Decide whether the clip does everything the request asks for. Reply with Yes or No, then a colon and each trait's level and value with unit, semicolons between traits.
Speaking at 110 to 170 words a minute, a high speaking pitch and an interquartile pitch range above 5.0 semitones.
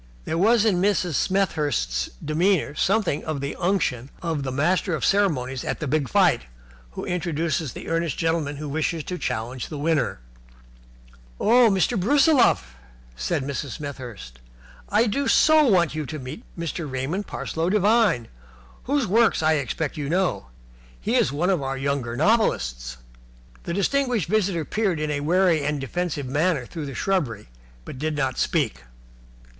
No: average, 155 wpm; medium, 160 Hz; wide, 5.6 semitones